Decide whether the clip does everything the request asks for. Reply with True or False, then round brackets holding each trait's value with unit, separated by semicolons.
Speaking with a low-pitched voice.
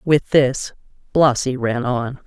True (130 Hz)